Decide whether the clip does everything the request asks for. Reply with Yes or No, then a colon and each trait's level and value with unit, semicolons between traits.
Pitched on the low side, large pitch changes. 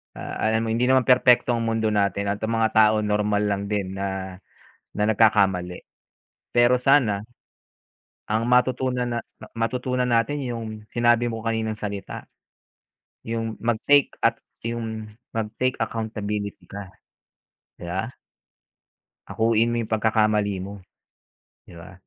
No: low, 110 Hz; narrow, 2.4 semitones